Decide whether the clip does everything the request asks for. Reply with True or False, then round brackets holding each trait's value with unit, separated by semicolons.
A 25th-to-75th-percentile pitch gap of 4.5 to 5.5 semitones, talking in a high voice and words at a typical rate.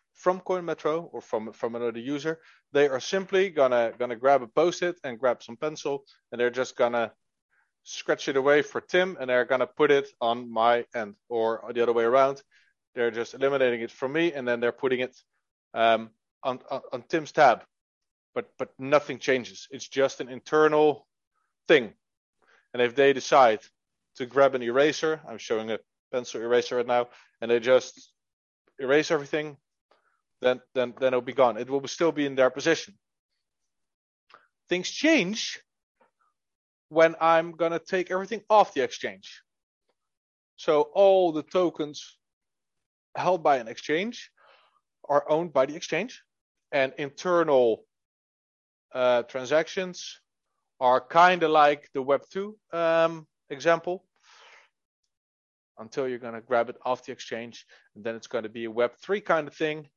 False (5.1 semitones; 140 Hz; 155 wpm)